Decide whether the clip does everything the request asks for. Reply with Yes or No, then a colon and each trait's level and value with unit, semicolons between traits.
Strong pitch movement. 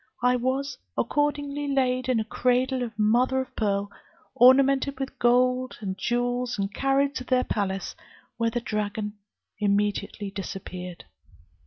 No: average, 3.9 semitones